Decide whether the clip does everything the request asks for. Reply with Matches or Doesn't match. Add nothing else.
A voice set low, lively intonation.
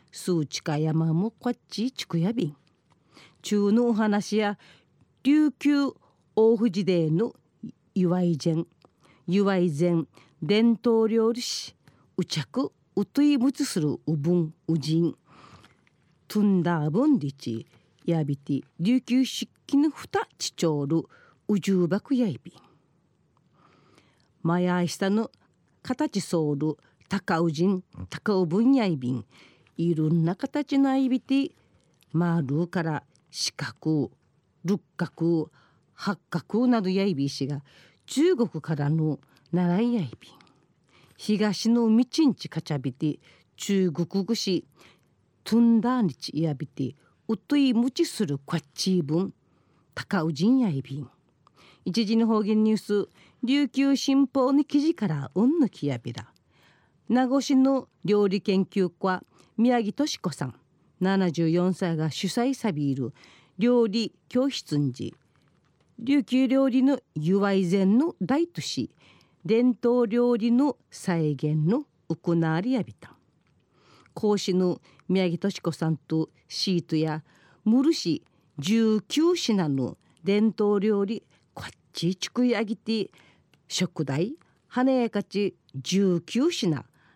Doesn't match